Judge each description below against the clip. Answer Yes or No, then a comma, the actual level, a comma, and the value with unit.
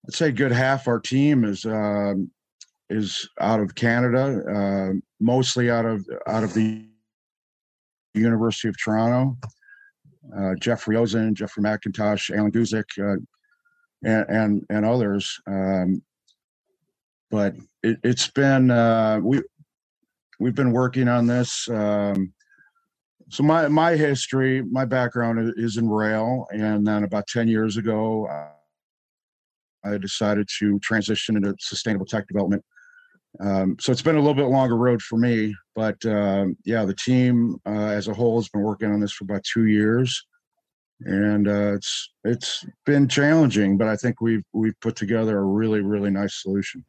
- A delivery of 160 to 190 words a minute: No, average, 150 wpm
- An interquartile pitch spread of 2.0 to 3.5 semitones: Yes, average, 3.2 semitones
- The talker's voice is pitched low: Yes, low, 110 Hz